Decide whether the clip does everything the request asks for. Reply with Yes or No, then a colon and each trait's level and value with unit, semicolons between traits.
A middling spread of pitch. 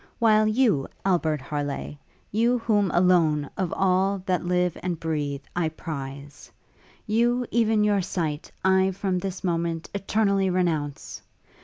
Yes: average, 4.2 semitones